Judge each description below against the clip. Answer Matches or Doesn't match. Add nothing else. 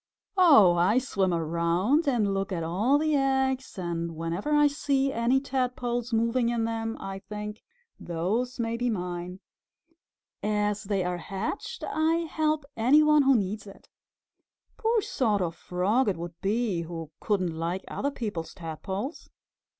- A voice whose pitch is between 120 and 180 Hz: Doesn't match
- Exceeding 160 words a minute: Doesn't match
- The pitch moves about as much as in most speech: Doesn't match